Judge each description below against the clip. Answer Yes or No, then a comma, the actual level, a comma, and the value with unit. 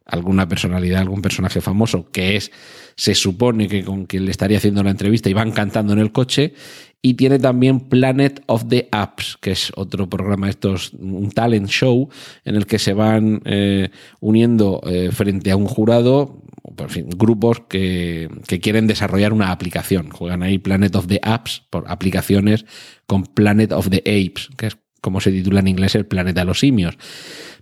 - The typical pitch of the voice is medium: No, low, 100 Hz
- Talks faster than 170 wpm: Yes, average, 185 wpm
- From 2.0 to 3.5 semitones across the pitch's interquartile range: Yes, narrow, 2.6 semitones